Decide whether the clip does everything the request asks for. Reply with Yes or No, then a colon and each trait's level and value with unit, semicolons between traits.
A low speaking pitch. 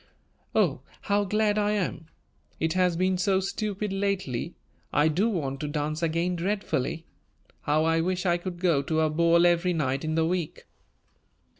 No: medium, 175 Hz